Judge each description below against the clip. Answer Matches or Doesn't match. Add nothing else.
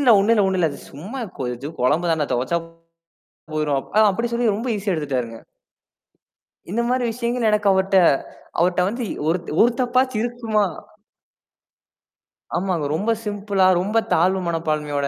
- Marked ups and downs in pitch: Matches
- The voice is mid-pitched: Doesn't match